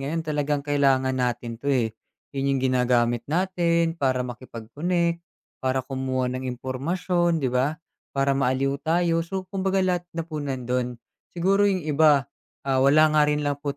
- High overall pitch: No, medium, 140 Hz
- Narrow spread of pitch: No, average, 4.4 semitones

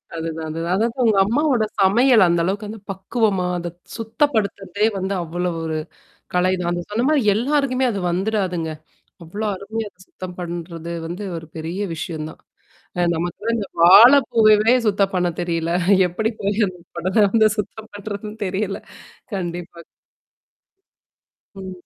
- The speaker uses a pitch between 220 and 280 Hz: No, high, 195 Hz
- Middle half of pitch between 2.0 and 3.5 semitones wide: No, average, 3.9 semitones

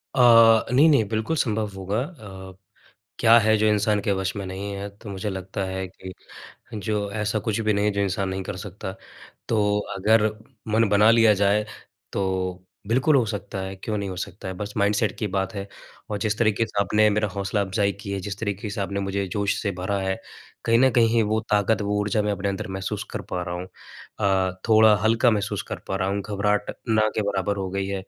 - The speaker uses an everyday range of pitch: No, narrow, 1.9 semitones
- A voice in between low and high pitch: No, low, 100 Hz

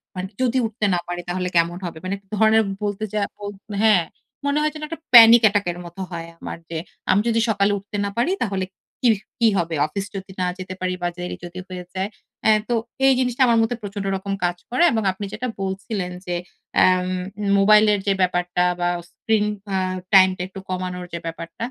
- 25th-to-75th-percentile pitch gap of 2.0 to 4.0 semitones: Yes, average, 3.3 semitones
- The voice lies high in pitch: Yes, high, 195 Hz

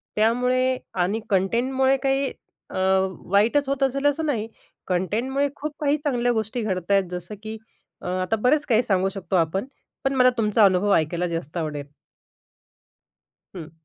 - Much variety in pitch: Yes, wide, 6.1 semitones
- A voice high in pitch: Yes, high, 220 Hz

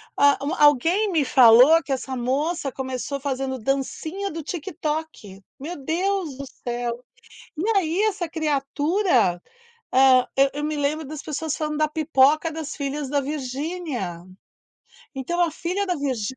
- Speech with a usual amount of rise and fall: Yes, average, 3.5 semitones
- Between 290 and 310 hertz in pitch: Yes, very high, 295 Hz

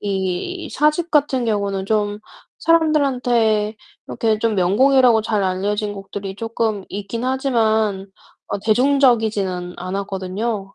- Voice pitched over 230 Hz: No, high, 215 Hz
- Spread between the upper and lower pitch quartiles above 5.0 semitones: No, average, 4.1 semitones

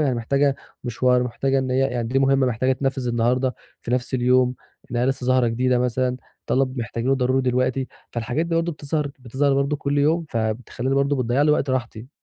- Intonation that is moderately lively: No, narrow, 1.8 semitones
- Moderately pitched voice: No, low, 130 Hz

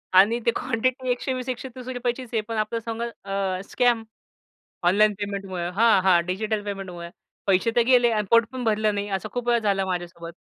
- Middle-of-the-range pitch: No, high, 215 Hz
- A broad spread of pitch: No, average, 3.7 semitones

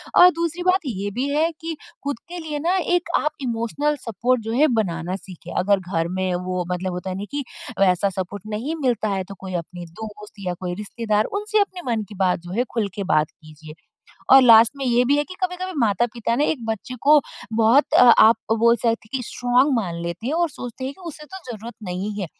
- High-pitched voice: Yes, high, 230 Hz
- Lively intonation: Yes, wide, 7.1 semitones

